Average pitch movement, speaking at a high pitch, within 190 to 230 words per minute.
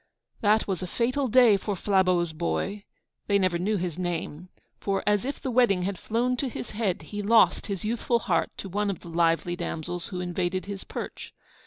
Yes: average, 3.4 semitones; high, 195 Hz; average, 195 wpm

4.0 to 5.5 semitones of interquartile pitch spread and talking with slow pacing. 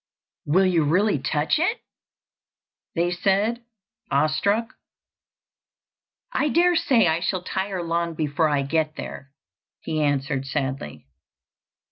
Yes: average, 5.1 semitones; slow, 110 wpm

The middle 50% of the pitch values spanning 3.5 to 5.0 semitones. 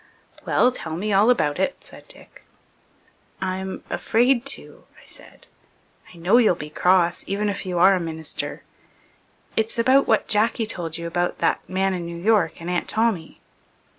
Yes: average, 4.4 semitones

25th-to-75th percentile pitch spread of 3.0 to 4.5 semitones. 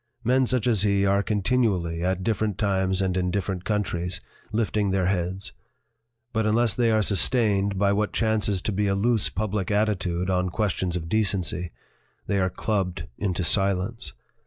No: narrow, 2.6 semitones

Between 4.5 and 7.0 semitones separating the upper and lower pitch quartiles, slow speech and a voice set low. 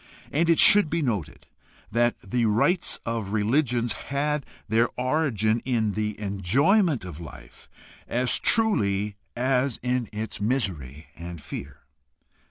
Yes: average, 5.2 semitones; slow, 125 wpm; low, 115 Hz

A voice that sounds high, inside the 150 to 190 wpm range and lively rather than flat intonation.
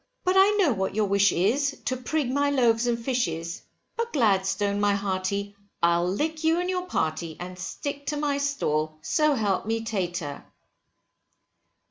Yes: high, 225 Hz; average, 160 wpm; wide, 7.1 semitones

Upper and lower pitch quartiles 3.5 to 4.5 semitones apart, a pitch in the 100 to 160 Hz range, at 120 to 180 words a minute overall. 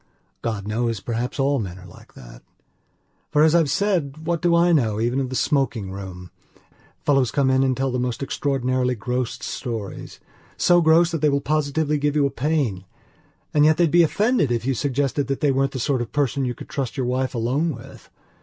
No: average, 3.8 semitones; low, 135 Hz; average, 200 wpm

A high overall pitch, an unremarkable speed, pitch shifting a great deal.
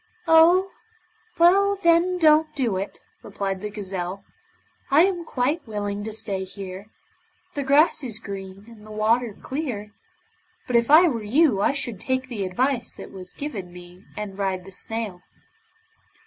Yes: high, 225 Hz; average, 155 wpm; wide, 7.2 semitones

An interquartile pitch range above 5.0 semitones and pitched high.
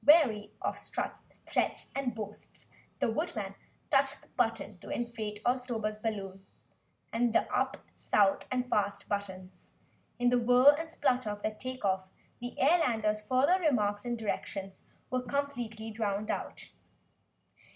No: average, 3.5 semitones; high, 225 Hz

